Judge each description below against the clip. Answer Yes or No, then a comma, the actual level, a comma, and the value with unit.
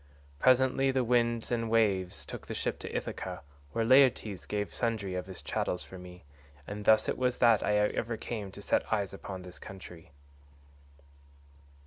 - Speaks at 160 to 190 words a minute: Yes, average, 165 wpm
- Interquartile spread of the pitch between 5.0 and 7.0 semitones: No, average, 3.7 semitones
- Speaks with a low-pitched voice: Yes, low, 105 Hz